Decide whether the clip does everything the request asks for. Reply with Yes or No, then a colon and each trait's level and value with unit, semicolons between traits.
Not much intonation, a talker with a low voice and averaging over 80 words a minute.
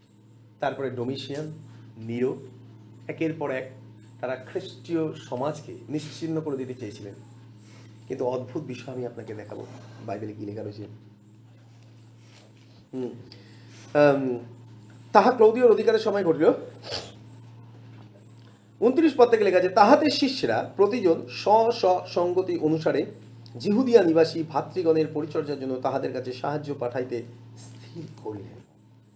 No: wide, 5.4 semitones; low, 125 Hz; average, 95 wpm